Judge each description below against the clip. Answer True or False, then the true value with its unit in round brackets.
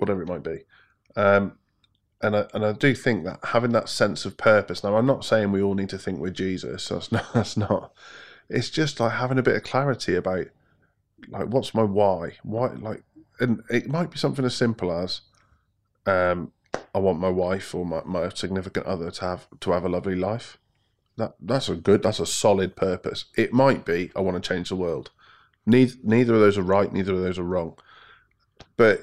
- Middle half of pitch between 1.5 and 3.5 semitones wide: False (4.0 semitones)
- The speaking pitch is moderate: False (100 Hz)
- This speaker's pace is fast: True (210 wpm)